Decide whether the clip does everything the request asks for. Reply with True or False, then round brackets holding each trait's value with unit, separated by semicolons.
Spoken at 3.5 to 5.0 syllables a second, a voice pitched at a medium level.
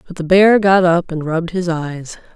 True (4.9 syllables/s; 175 Hz)